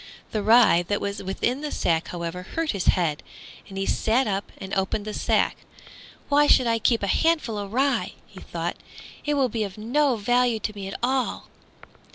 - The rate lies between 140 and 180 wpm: No, average, 195 wpm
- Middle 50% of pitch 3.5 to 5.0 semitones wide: Yes, average, 4.7 semitones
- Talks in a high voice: Yes, high, 220 Hz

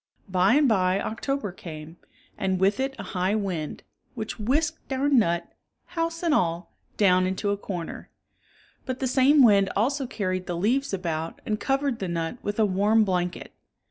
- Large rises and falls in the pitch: Yes, wide, 6.2 semitones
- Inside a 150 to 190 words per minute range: Yes, average, 170 wpm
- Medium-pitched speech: No, high, 205 Hz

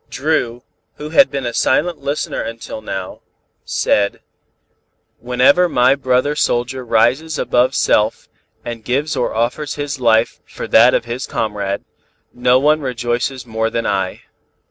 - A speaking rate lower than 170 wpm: Yes, average, 140 wpm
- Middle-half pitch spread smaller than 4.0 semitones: Yes, average, 3.6 semitones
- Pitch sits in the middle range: No, low, 125 Hz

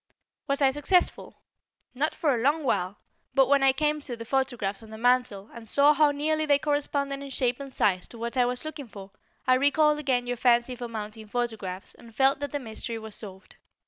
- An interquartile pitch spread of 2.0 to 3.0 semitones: No, average, 4.0 semitones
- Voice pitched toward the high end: Yes, very high, 255 Hz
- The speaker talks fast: Yes, fast, 210 wpm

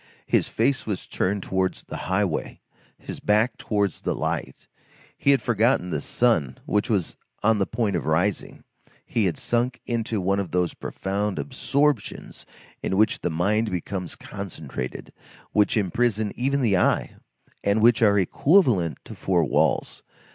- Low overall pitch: Yes, low, 105 Hz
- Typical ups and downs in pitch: Yes, average, 3.9 semitones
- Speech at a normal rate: Yes, average, 150 wpm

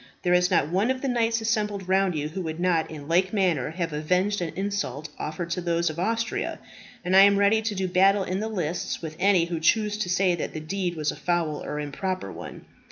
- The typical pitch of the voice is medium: Yes, medium, 180 Hz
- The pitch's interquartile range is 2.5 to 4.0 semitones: Yes, average, 3.4 semitones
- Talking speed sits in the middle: No, fast, 230 wpm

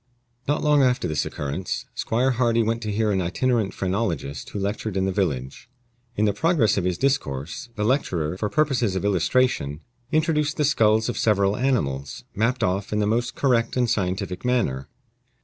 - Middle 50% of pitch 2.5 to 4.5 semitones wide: No, average, 5.2 semitones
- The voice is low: Yes, low, 105 Hz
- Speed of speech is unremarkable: Yes, average, 175 wpm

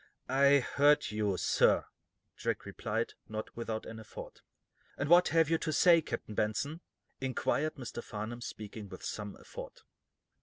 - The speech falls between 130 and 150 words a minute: Yes, average, 145 wpm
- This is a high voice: No, low, 120 Hz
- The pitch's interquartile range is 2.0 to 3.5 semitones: No, wide, 5.5 semitones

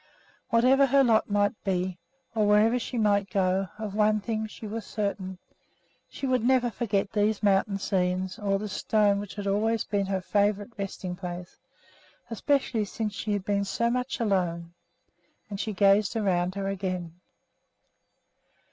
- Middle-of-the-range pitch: No, high, 205 Hz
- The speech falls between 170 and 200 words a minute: No, average, 155 wpm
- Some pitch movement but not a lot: No, narrow, 2.2 semitones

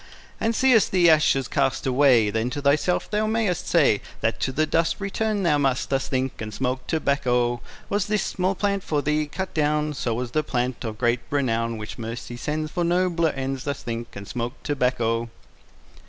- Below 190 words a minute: No, average, 195 wpm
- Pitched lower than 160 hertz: Yes, medium, 140 Hz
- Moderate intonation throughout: No, wide, 5.7 semitones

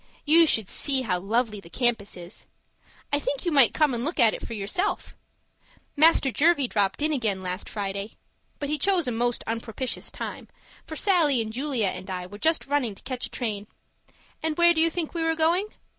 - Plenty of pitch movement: Yes, wide, 6.9 semitones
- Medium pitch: No, very high, 255 Hz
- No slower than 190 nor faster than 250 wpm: Yes, fast, 205 wpm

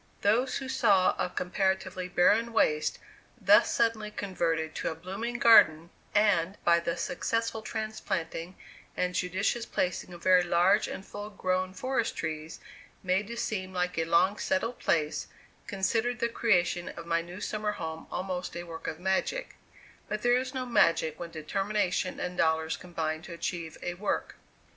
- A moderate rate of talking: Yes, average, 160 wpm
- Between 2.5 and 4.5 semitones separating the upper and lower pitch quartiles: Yes, average, 4.1 semitones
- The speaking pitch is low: No, medium, 185 Hz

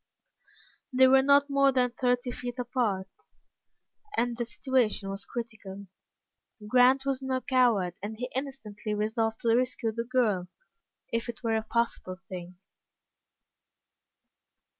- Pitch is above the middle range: Yes, high, 235 Hz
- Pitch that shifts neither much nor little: Yes, average, 3.3 semitones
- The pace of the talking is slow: Yes, slow, 125 wpm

